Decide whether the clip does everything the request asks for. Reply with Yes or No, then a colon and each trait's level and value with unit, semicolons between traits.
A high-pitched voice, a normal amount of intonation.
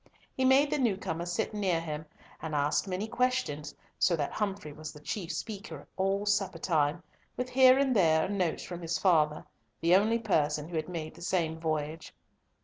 No: medium, 175 Hz; average, 4.7 semitones